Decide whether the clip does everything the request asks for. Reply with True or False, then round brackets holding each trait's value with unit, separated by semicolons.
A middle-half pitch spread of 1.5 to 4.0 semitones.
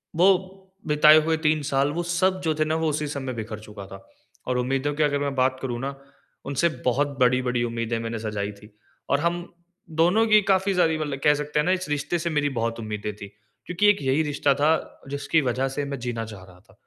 False (5.0 semitones)